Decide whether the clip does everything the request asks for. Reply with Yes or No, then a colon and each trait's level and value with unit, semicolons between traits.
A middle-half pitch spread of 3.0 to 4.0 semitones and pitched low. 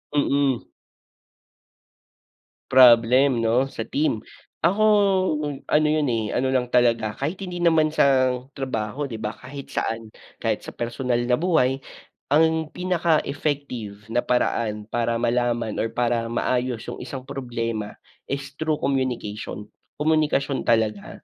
Yes: average, 3.7 semitones; low, 125 Hz